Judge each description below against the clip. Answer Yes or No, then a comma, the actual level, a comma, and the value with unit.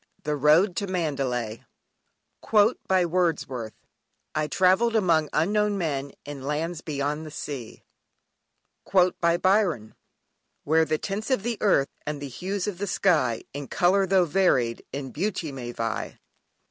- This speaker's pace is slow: Yes, slow, 125 wpm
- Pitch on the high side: No, medium, 160 Hz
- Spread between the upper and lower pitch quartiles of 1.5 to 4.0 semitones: No, average, 5.1 semitones